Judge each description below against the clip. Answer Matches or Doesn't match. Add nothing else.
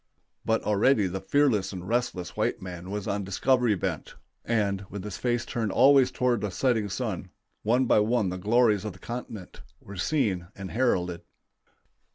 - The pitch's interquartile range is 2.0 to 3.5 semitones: Doesn't match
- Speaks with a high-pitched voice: Doesn't match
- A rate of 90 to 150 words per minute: Doesn't match